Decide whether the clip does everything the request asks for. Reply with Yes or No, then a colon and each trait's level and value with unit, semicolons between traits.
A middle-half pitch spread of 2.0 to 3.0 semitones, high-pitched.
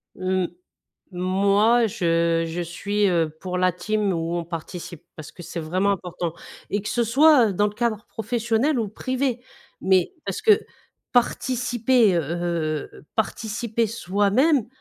No: average, 5.1 semitones; high, 200 Hz